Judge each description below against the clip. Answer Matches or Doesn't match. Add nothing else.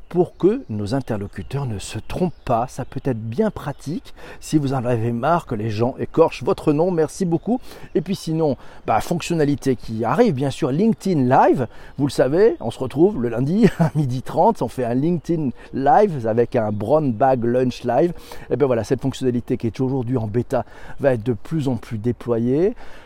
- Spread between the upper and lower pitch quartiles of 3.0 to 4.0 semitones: Doesn't match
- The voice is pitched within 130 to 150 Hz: Matches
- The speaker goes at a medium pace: Matches